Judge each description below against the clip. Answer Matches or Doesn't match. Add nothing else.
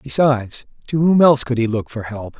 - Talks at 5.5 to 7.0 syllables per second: Matches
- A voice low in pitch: Matches